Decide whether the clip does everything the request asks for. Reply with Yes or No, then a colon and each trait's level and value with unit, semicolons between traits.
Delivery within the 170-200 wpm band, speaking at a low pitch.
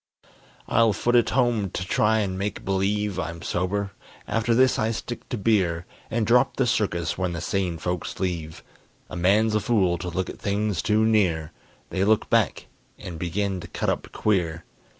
Yes: average, 180 wpm; low, 100 Hz